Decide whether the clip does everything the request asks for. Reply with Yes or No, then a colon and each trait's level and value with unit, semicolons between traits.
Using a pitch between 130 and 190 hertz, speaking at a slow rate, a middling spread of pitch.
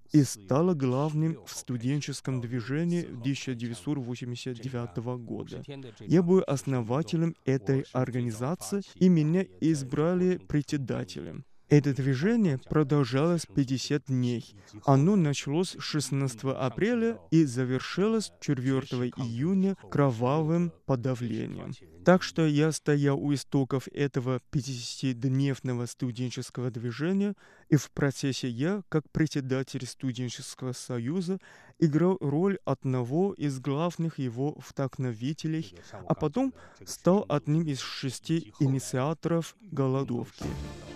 Yes: medium, 140 Hz; slow, 95 wpm; average, 4.0 semitones